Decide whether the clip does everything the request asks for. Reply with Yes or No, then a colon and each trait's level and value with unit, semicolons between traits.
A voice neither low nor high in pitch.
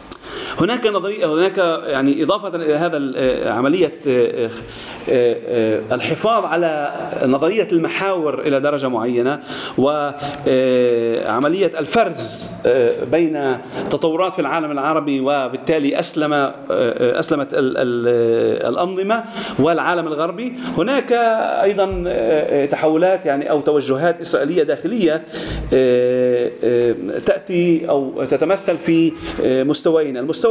Yes: medium, 160 Hz